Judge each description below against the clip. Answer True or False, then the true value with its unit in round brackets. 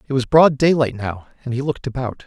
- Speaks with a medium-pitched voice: False (130 Hz)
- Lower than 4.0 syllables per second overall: False (6.1 syllables/s)